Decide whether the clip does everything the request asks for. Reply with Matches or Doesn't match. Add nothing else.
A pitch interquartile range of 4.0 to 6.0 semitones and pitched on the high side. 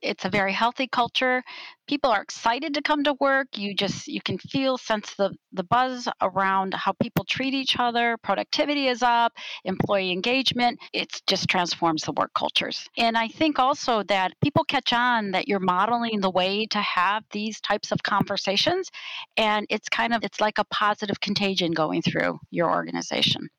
Matches